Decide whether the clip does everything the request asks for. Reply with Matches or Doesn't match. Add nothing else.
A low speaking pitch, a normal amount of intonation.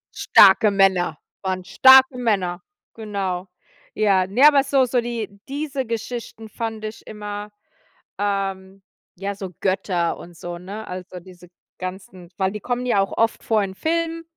Doesn't match